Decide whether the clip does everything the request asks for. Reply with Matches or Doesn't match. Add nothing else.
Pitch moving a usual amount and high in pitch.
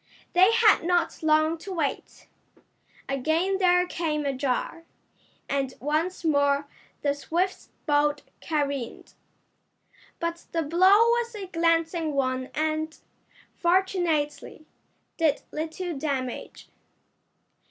Matches